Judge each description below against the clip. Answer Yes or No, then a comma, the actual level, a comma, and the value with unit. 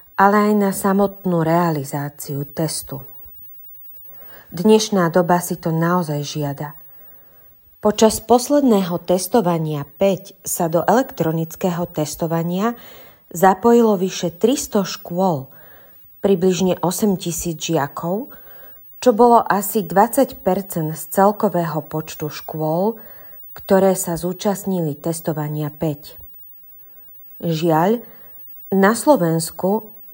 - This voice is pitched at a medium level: Yes, medium, 180 Hz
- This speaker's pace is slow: Yes, slow, 85 wpm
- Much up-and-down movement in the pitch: No, average, 4.3 semitones